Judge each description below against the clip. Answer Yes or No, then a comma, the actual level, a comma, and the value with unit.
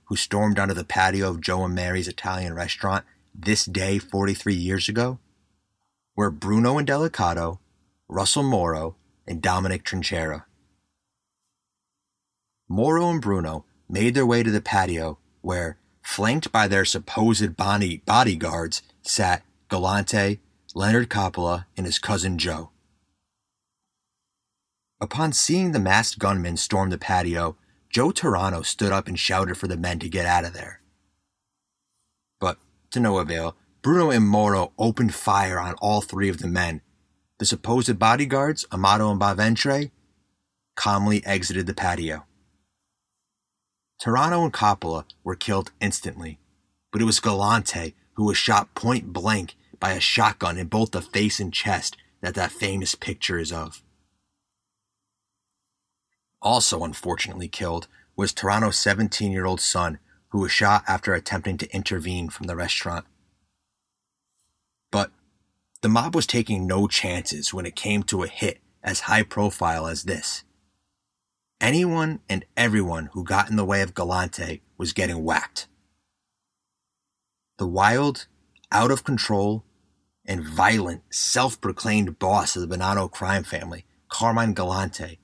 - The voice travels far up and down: No, average, 3.0 semitones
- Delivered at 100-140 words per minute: Yes, slow, 135 wpm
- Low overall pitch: Yes, very low, 95 Hz